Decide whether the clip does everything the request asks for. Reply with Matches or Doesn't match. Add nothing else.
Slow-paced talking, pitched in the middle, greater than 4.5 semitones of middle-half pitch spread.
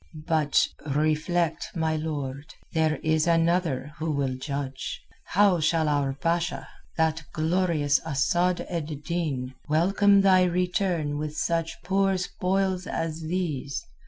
Doesn't match